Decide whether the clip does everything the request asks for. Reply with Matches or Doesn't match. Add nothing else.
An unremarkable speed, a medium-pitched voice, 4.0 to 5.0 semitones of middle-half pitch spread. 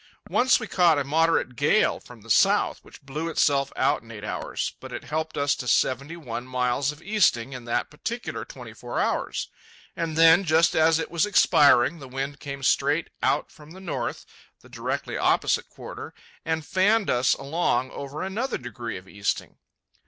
Matches